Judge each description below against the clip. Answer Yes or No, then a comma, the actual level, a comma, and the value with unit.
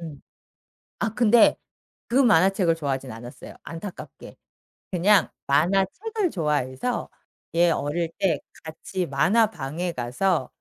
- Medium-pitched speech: Yes, medium, 170 Hz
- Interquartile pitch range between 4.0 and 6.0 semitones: Yes, average, 5.2 semitones